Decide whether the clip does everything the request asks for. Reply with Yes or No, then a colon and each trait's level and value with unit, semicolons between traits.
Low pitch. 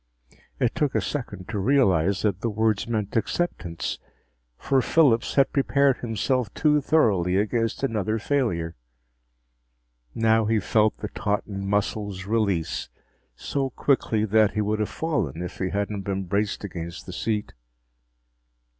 Yes: low, 105 Hz